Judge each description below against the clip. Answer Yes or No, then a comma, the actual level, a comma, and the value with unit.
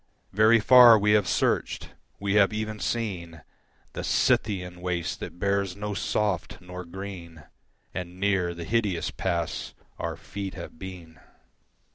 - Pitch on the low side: Yes, very low, 95 Hz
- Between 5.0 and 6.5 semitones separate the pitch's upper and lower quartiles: No, average, 3.0 semitones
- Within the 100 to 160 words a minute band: Yes, slow, 135 wpm